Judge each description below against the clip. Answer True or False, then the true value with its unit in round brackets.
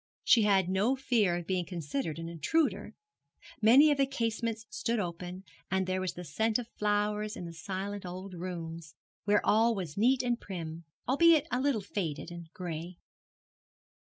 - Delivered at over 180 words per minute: False (165 wpm)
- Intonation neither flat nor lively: True (4.8 semitones)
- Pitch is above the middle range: True (195 Hz)